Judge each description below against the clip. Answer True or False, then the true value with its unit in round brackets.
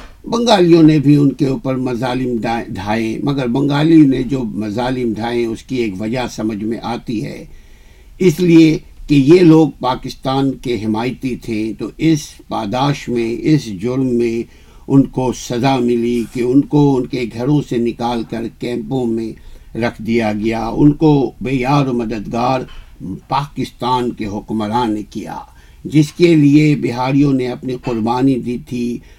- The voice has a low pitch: True (125 Hz)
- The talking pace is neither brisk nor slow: True (155 wpm)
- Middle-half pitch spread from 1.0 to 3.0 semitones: False (3.4 semitones)